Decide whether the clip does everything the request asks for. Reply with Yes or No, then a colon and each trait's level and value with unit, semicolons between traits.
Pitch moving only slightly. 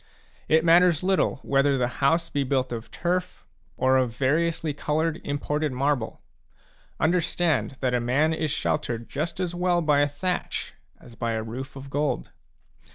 No: average, 4.1 semitones